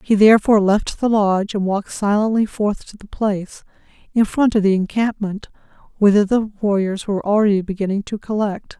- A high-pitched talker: Yes, high, 205 Hz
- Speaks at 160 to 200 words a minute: Yes, average, 170 wpm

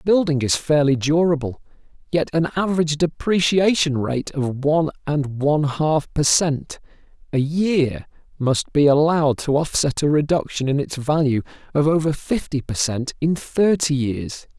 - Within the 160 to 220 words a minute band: No, average, 150 wpm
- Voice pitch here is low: No, medium, 150 Hz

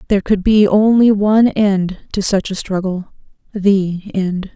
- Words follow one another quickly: No, average, 145 wpm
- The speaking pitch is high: Yes, high, 200 Hz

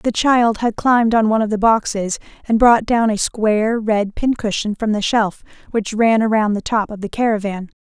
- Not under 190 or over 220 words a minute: Yes, fast, 205 wpm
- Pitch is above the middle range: Yes, high, 220 Hz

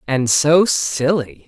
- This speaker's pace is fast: No, slow, 120 wpm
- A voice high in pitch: No, medium, 140 Hz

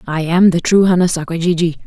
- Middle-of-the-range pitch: Yes, medium, 170 Hz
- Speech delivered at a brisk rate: Yes, fast, 225 wpm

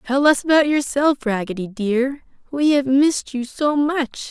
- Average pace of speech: Yes, average, 165 wpm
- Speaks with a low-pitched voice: No, very high, 270 Hz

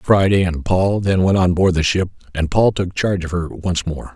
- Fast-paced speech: Yes, fast, 245 wpm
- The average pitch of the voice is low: Yes, very low, 90 Hz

